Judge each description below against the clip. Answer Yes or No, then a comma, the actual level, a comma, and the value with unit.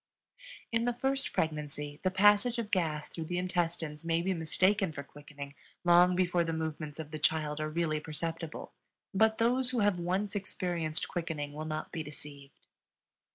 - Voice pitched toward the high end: No, medium, 165 Hz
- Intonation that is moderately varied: Yes, average, 3.7 semitones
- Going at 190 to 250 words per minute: No, average, 165 wpm